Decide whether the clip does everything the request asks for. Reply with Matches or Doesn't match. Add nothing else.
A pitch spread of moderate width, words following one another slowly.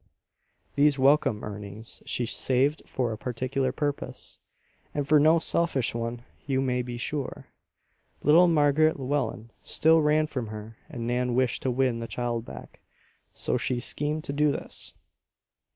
Doesn't match